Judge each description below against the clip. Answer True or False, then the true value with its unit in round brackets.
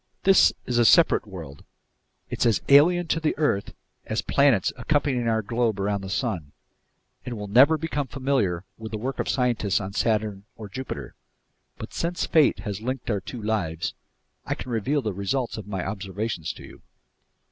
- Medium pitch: False (110 Hz)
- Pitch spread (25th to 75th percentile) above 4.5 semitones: True (5.1 semitones)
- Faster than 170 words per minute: True (180 wpm)